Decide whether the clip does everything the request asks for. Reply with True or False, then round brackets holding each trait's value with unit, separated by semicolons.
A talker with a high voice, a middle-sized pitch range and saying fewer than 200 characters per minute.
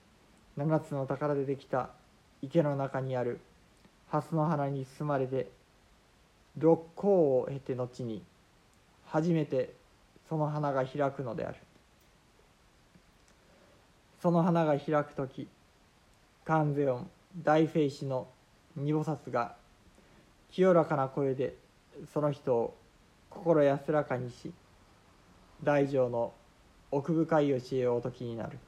False (140 Hz; 3.2 semitones; 190 characters per minute)